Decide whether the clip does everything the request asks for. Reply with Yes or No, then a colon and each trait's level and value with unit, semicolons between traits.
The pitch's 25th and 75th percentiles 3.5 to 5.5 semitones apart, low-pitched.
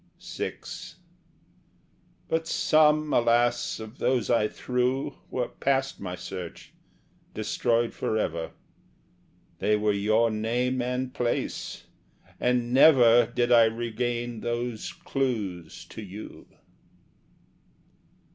No: narrow, 2.5 semitones; low, 120 Hz